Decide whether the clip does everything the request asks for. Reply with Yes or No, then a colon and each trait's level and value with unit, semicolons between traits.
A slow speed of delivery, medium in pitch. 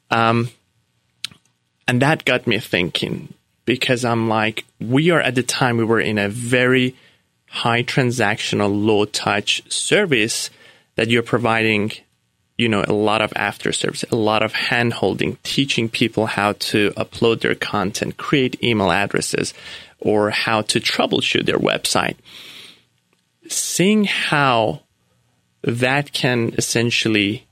No: slow, 130 wpm; low, 115 Hz